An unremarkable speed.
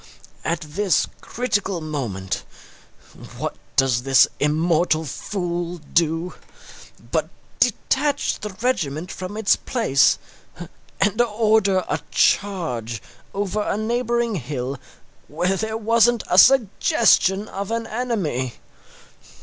No: slow, 100 wpm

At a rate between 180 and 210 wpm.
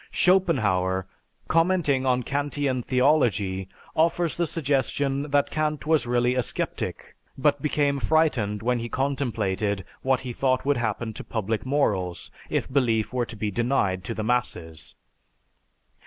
No: average, 140 wpm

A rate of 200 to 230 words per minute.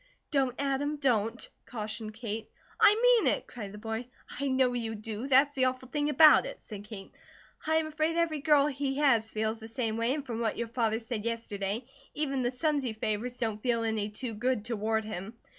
Yes: fast, 205 wpm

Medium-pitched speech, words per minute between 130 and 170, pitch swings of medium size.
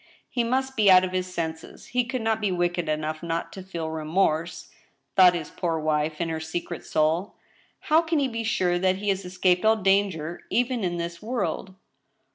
No: medium, 180 Hz; fast, 205 wpm; average, 4.7 semitones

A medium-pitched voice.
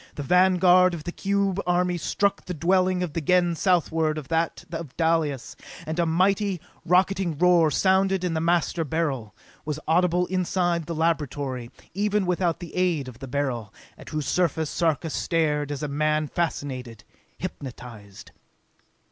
Yes: medium, 165 Hz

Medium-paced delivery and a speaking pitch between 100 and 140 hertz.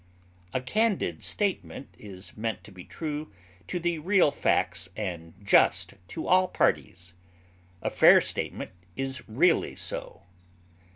No: slow, 125 wpm; low, 135 Hz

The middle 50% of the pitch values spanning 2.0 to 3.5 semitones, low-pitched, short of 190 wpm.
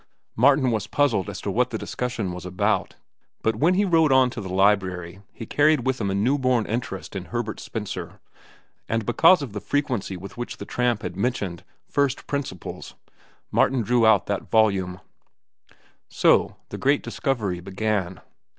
No: average, 5.2 semitones; low, 110 Hz; average, 170 wpm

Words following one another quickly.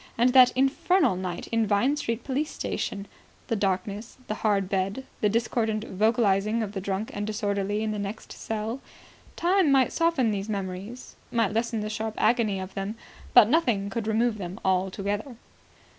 No: average, 165 wpm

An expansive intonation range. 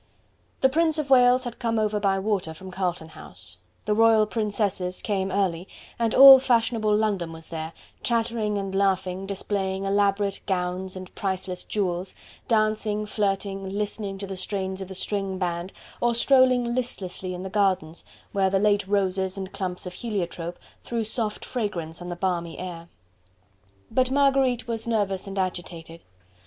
No: average, 3.0 semitones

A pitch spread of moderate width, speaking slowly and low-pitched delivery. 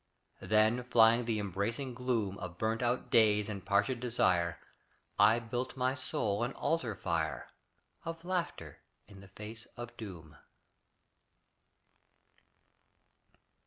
Yes: average, 3.7 semitones; slow, 115 wpm; low, 110 Hz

